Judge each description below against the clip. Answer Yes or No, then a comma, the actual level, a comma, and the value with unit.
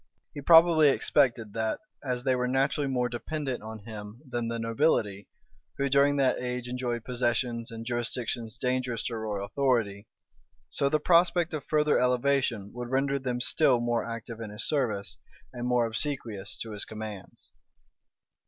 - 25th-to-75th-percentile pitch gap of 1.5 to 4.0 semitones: Yes, average, 3.1 semitones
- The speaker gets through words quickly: No, average, 160 wpm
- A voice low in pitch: Yes, low, 125 Hz